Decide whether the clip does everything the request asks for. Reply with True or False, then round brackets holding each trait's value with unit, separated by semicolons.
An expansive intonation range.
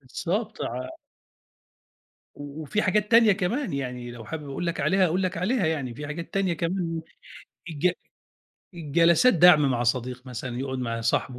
True (6.2 semitones)